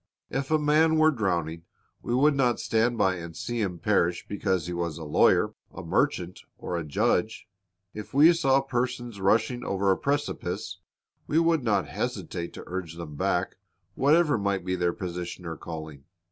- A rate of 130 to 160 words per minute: No, average, 175 wpm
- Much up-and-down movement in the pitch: Yes, wide, 7.3 semitones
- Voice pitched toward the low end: Yes, low, 100 Hz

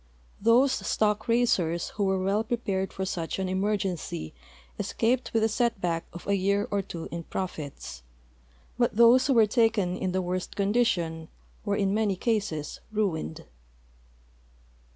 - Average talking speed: Yes, average, 150 wpm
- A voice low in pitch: No, high, 200 Hz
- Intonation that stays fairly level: No, average, 4.0 semitones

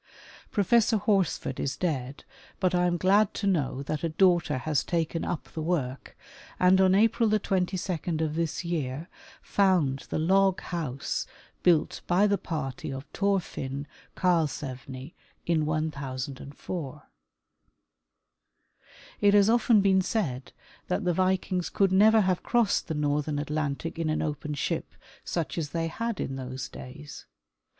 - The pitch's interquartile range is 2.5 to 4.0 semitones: No, average, 4.8 semitones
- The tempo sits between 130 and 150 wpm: Yes, average, 140 wpm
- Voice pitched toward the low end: No, medium, 165 Hz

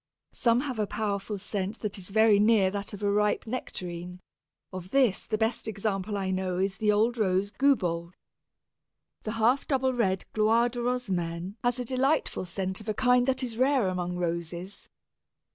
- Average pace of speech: Yes, average, 175 wpm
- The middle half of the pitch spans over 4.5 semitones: No, average, 4.2 semitones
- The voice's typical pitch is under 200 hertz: No, high, 210 Hz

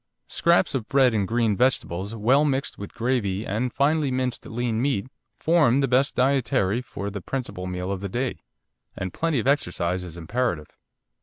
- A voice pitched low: Yes, low, 120 Hz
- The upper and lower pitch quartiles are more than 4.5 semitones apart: Yes, average, 5.3 semitones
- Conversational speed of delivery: Yes, average, 170 wpm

